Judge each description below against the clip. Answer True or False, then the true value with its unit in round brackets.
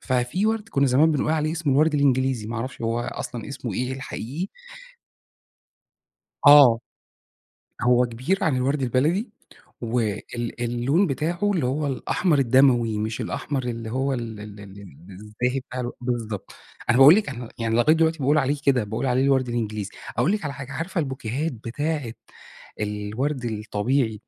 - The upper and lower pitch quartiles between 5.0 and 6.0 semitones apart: False (4.0 semitones)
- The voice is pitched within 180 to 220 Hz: False (130 Hz)